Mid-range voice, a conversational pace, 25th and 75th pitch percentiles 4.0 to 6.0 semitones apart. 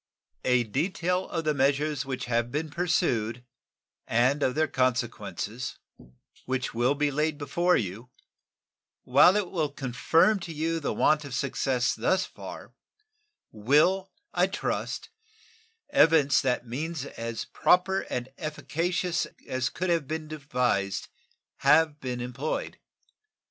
No: medium, 145 Hz; slow, 130 wpm; average, 4.7 semitones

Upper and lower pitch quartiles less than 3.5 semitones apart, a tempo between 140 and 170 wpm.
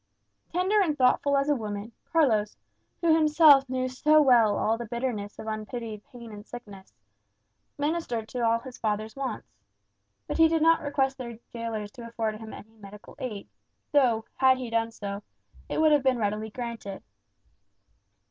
No: average, 4.3 semitones; average, 160 wpm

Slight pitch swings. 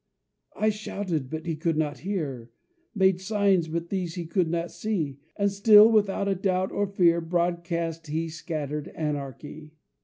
No: average, 3.7 semitones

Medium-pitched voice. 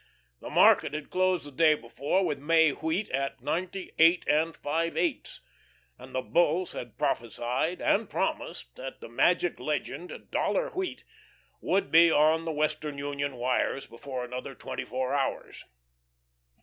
Yes: medium, 150 Hz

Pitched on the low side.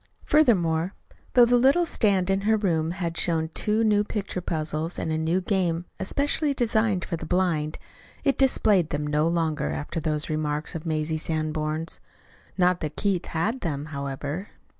No: medium, 170 Hz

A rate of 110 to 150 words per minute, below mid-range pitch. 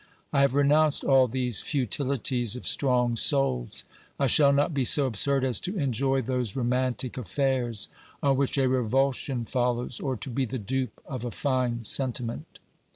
No: average, 160 wpm; low, 130 Hz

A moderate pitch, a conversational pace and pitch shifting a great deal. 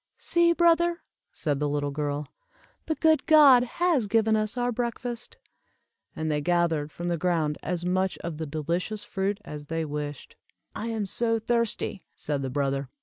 Yes: medium, 180 Hz; average, 165 wpm; wide, 7.9 semitones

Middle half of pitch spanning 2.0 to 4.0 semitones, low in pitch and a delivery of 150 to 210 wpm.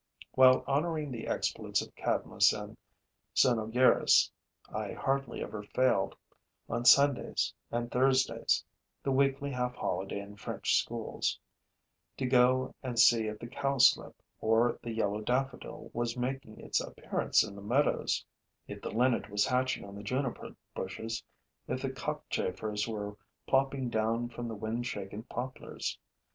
No: average, 3.1 semitones; low, 120 Hz; average, 140 wpm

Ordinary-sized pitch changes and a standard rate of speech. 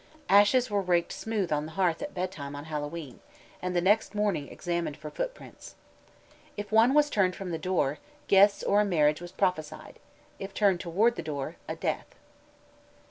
Yes: average, 4.5 semitones; average, 170 wpm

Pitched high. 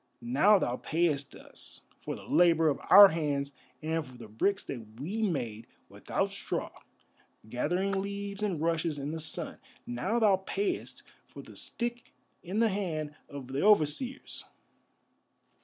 No: medium, 165 Hz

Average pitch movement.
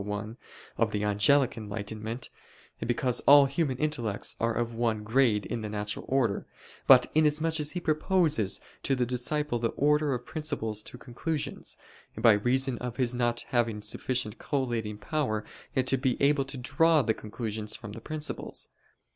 Yes: average, 4.6 semitones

